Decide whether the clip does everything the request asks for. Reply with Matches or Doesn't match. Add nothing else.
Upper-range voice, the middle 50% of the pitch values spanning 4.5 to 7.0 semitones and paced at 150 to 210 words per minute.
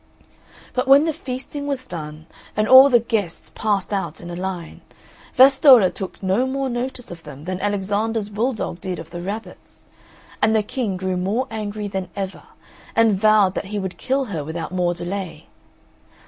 Matches